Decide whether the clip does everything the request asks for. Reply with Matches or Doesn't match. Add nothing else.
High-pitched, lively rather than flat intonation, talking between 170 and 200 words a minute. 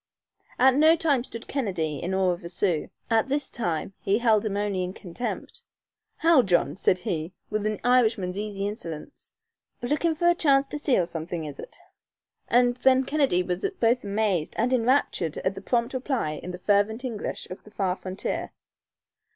Matches